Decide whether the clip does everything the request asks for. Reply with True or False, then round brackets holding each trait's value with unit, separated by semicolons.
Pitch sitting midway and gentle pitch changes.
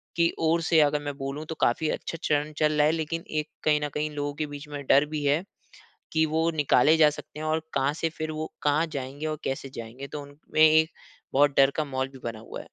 True (150 Hz; 1.9 semitones)